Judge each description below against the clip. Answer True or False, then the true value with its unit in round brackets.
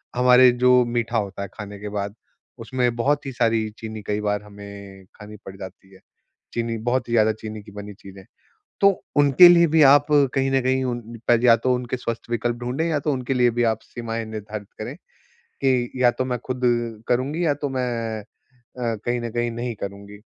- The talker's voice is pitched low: True (120 Hz)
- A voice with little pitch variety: False (3.2 semitones)